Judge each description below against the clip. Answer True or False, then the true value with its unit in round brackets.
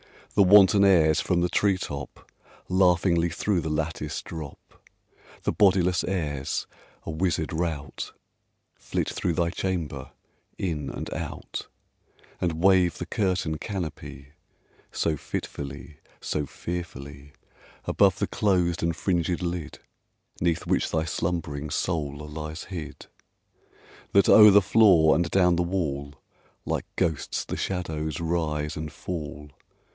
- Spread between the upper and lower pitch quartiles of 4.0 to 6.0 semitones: False (3.1 semitones)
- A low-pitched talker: True (85 Hz)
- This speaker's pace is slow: True (125 wpm)